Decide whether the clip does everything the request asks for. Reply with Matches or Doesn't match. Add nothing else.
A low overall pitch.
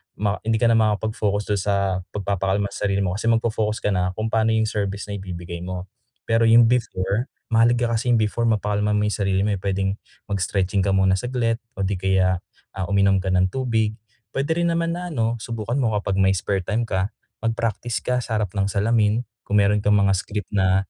Matches